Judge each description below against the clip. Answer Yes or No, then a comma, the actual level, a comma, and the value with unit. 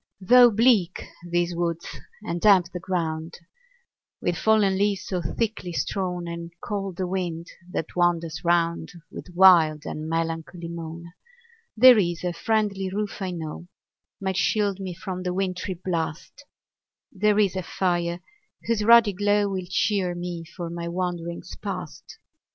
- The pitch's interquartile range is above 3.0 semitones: No, narrow, 2.6 semitones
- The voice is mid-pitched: Yes, medium, 180 Hz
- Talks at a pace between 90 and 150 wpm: Yes, average, 145 wpm